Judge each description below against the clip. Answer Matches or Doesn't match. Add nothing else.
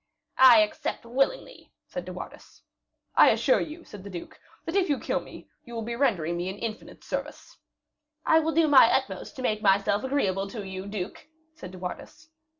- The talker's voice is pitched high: Matches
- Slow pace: Doesn't match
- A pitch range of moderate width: Doesn't match